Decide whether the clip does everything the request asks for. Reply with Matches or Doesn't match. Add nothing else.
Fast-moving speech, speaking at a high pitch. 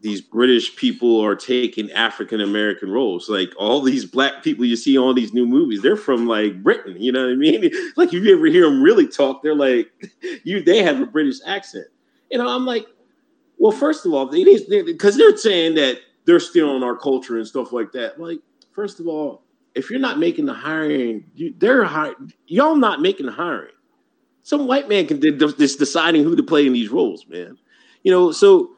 Matches